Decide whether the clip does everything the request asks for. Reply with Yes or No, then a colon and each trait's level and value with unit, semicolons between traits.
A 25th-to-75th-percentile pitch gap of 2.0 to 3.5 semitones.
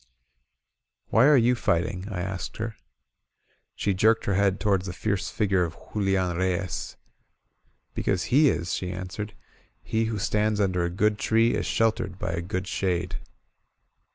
Yes: average, 3.0 semitones